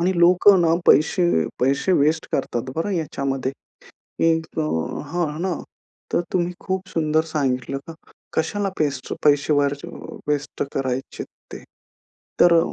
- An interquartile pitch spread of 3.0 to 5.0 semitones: Yes, average, 4.0 semitones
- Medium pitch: Yes, medium, 155 Hz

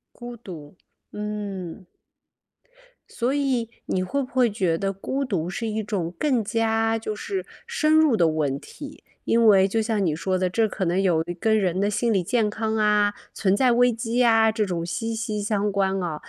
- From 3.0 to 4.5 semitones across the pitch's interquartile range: Yes, average, 3.4 semitones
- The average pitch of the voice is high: Yes, high, 210 Hz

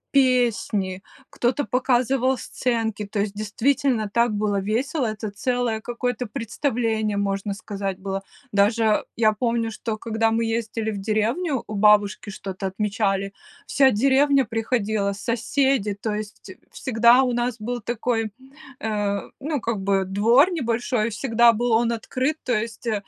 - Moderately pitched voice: No, high, 225 Hz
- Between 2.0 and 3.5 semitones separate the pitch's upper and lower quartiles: Yes, average, 2.9 semitones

